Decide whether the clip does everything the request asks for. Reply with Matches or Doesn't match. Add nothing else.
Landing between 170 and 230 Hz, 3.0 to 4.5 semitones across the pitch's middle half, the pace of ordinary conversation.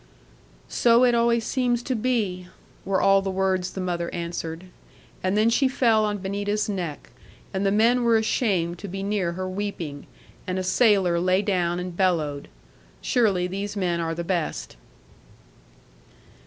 Matches